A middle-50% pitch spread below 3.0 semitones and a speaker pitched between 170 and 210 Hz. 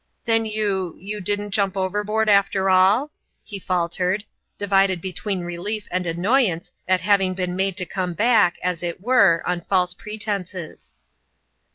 Yes: narrow, 2.5 semitones; high, 190 Hz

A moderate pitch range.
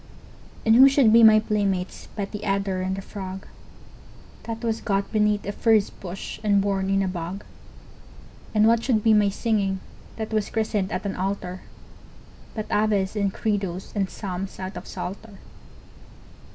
No: narrow, 2.1 semitones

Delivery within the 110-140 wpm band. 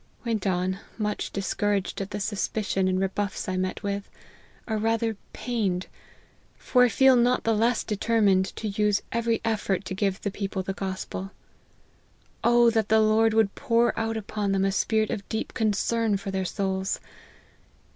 No: average, 170 wpm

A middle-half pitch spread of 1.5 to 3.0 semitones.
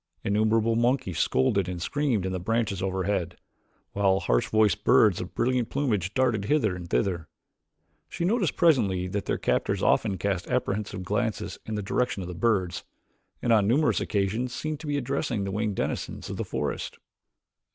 No: average, 4.3 semitones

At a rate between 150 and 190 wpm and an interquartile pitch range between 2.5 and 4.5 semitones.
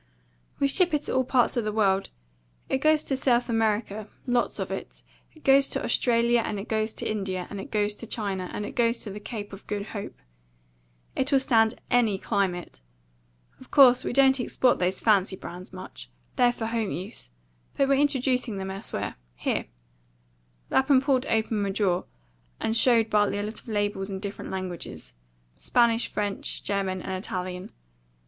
Yes: average, 175 wpm; average, 4.0 semitones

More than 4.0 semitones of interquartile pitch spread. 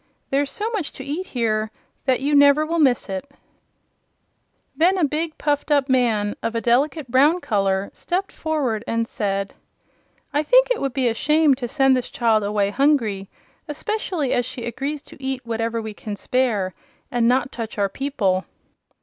Yes: average, 4.8 semitones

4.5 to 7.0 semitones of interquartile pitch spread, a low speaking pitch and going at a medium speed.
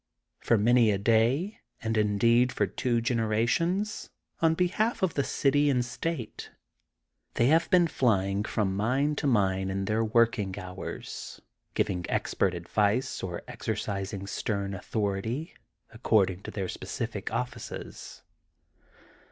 No: average, 4.9 semitones; low, 115 Hz; slow, 125 wpm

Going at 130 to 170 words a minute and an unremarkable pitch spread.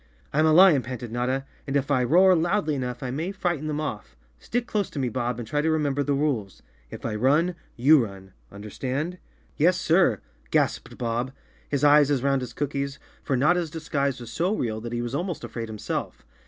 No: average, 200 wpm; average, 4.6 semitones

